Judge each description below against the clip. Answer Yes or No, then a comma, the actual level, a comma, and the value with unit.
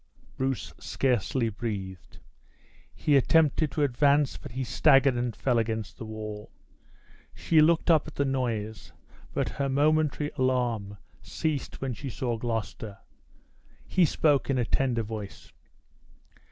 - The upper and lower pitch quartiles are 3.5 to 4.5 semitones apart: Yes, average, 4.1 semitones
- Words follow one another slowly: Yes, slow, 130 wpm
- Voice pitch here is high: No, low, 130 Hz